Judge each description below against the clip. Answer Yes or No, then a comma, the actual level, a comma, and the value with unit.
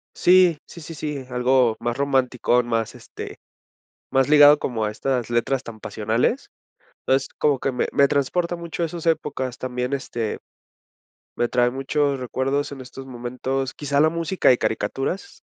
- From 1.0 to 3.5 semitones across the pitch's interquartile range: Yes, average, 3.1 semitones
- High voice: No, low, 135 Hz